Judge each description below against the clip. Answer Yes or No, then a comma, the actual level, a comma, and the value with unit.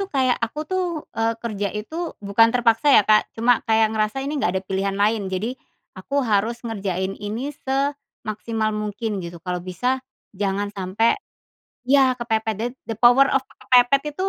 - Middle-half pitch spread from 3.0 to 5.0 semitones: Yes, average, 3.5 semitones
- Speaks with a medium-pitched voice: No, high, 225 Hz